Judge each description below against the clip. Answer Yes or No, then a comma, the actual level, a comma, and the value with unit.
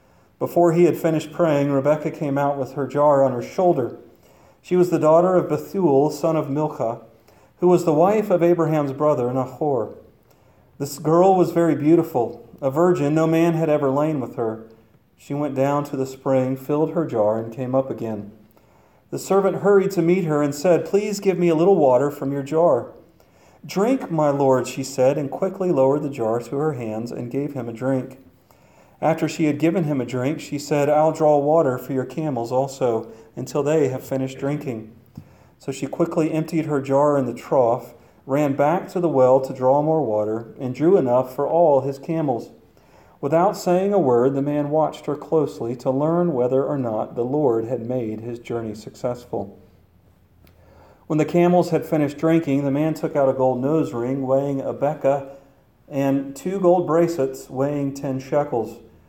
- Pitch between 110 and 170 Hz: Yes, medium, 140 Hz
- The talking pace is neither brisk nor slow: Yes, average, 185 wpm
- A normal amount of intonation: Yes, average, 3.8 semitones